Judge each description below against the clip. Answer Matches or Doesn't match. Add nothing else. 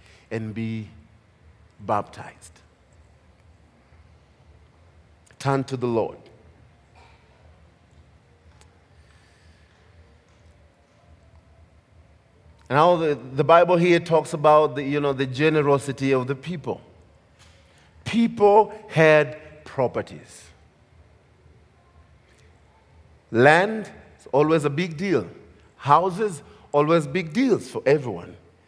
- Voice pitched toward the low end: Matches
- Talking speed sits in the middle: Doesn't match